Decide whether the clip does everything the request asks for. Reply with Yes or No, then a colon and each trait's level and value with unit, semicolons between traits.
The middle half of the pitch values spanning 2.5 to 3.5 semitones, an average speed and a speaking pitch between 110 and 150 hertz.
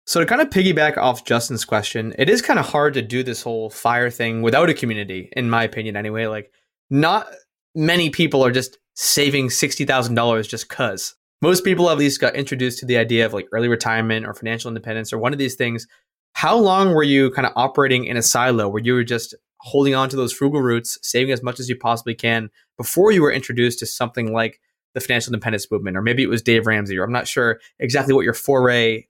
No: average, 3.0 semitones; fast, 225 wpm; low, 120 Hz